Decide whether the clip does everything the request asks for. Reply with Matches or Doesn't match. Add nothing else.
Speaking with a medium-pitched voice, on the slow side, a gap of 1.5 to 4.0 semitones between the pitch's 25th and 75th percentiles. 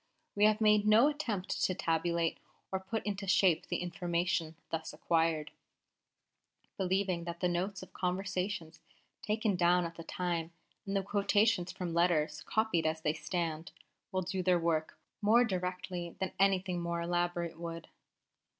Doesn't match